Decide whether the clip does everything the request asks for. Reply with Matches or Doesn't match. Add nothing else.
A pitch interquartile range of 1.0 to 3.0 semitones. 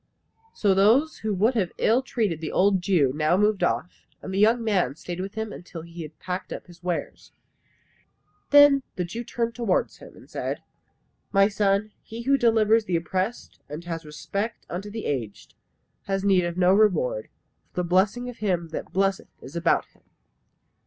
Doesn't match